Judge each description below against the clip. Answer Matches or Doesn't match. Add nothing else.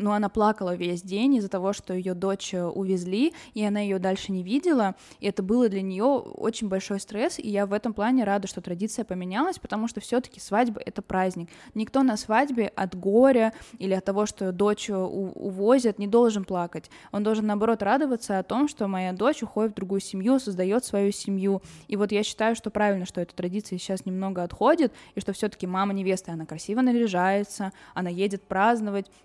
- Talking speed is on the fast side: Matches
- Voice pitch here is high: Matches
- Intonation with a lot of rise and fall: Doesn't match